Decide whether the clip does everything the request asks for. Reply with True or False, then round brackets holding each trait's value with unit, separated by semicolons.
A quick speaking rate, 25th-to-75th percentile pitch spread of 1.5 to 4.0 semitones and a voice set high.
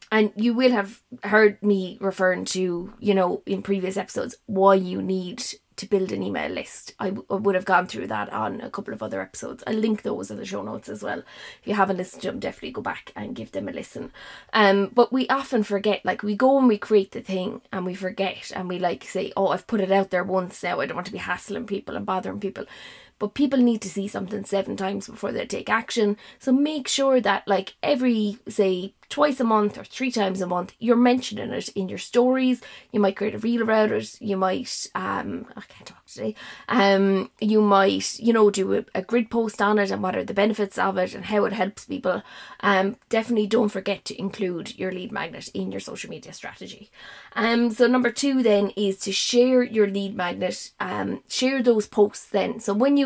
True (225 wpm; 3.1 semitones; 205 Hz)